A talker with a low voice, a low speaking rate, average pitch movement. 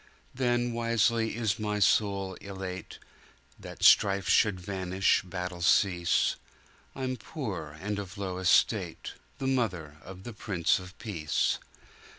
Yes: low, 100 Hz; slow, 115 wpm; average, 3.6 semitones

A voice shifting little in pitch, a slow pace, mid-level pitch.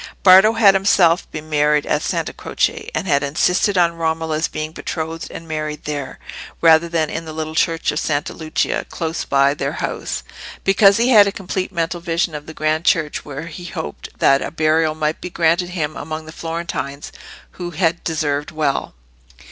No: narrow, 2.0 semitones; average, 180 wpm; medium, 160 Hz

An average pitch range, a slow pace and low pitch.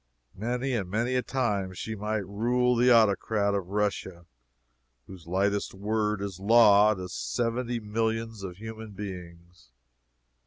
Yes: average, 3.0 semitones; slow, 130 wpm; low, 105 Hz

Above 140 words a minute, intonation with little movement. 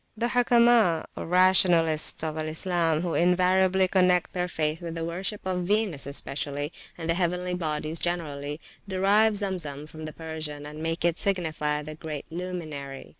No: average, 160 wpm; average, 3.0 semitones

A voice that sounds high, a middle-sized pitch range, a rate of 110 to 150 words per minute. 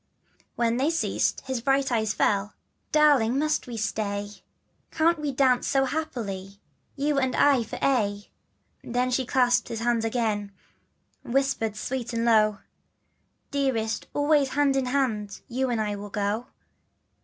Yes: high, 245 Hz; average, 4.0 semitones; average, 145 wpm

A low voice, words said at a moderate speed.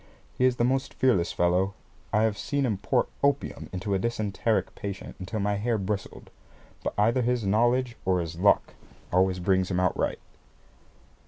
Yes: low, 105 Hz; average, 170 wpm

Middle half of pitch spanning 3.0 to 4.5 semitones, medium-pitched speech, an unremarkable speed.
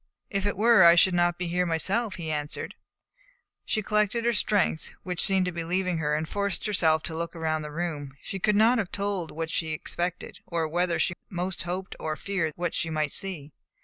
No: average, 3.3 semitones; medium, 175 Hz; fast, 210 wpm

